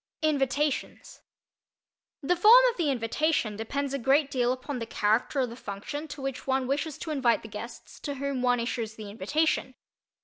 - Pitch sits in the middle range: No, very high, 270 Hz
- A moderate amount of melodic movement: Yes, average, 3.9 semitones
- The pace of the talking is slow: No, average, 175 wpm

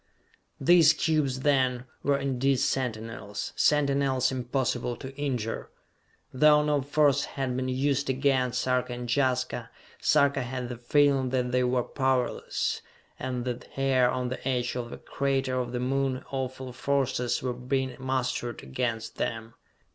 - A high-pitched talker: No, low, 130 Hz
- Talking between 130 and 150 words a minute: Yes, average, 140 wpm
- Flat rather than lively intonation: Yes, narrow, 1.7 semitones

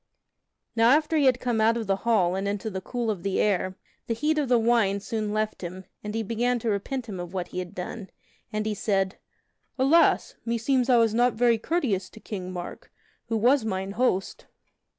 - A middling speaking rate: No, fast, 210 wpm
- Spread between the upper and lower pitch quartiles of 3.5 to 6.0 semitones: Yes, average, 3.8 semitones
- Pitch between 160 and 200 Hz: No, high, 220 Hz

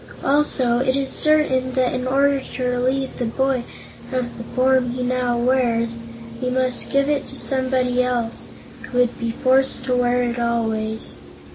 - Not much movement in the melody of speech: Yes, narrow, 1.5 semitones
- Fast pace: No, average, 165 wpm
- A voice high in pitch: Yes, very high, 255 Hz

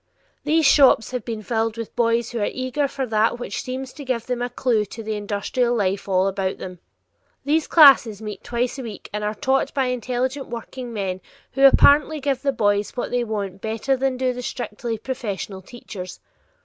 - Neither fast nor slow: Yes, average, 190 wpm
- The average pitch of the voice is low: No, high, 240 Hz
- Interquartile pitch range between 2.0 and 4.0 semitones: Yes, average, 3.7 semitones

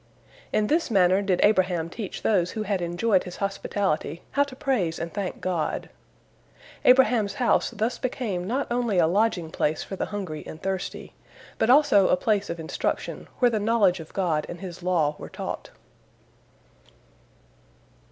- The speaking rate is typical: Yes, average, 160 wpm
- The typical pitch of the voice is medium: No, high, 195 Hz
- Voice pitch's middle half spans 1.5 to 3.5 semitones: No, average, 4.2 semitones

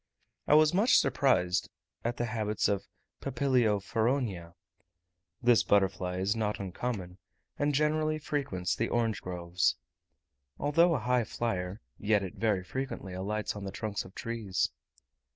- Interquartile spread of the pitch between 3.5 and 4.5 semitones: No, average, 5.1 semitones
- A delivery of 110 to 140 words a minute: Yes, slow, 135 wpm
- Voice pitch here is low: Yes, low, 110 Hz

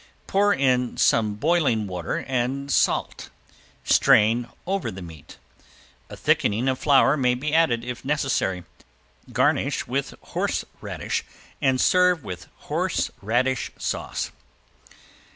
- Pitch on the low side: Yes, low, 130 Hz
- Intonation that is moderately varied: Yes, average, 4.3 semitones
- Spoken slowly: Yes, slow, 110 wpm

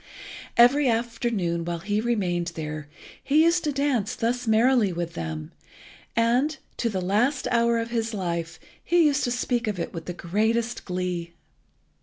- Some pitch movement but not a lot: No, wide, 5.8 semitones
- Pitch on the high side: Yes, high, 225 Hz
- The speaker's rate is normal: Yes, average, 160 wpm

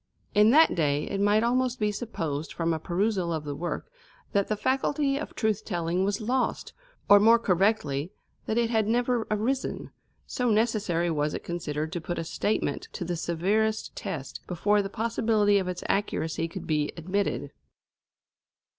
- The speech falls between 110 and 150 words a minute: No, average, 165 wpm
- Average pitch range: Yes, average, 4.9 semitones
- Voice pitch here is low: No, high, 200 Hz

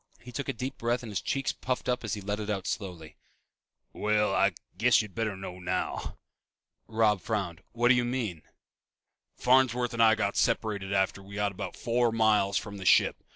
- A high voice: No, low, 110 Hz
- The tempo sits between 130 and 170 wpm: No, average, 190 wpm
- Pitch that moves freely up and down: No, average, 3.5 semitones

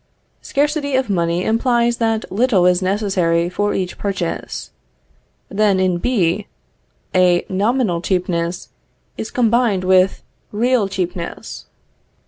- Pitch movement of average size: Yes, average, 4.3 semitones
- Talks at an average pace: No, slow, 110 wpm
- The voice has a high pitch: Yes, high, 195 Hz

